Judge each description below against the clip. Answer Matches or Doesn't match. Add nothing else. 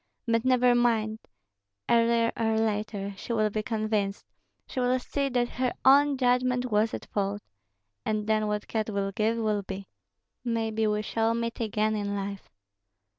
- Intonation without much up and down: Matches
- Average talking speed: Matches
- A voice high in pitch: Matches